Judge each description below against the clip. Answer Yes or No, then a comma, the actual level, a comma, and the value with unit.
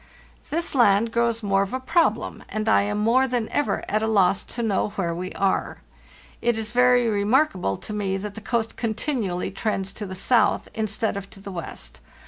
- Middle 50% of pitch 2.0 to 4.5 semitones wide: Yes, average, 3.2 semitones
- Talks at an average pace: Yes, average, 195 wpm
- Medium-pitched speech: No, high, 215 Hz